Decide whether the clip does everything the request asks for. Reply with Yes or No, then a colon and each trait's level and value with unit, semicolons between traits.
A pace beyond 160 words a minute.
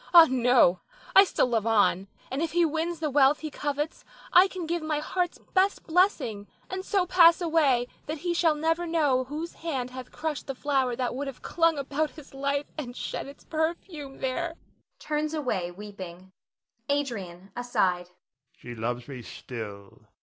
Yes: average, 170 wpm